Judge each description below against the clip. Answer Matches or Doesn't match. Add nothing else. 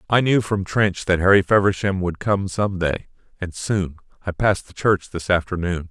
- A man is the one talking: Matches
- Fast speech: Doesn't match